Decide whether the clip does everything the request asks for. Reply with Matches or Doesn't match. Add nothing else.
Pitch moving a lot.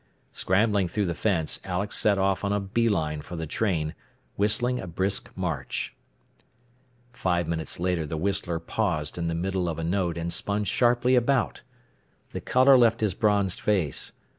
Doesn't match